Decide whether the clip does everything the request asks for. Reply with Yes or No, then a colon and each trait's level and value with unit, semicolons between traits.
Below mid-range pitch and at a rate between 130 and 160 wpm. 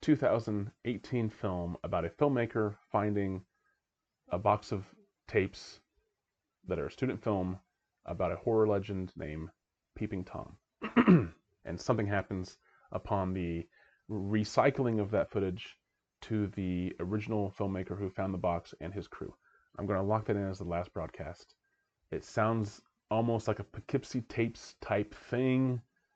Yes: low, 105 Hz; average, 140 wpm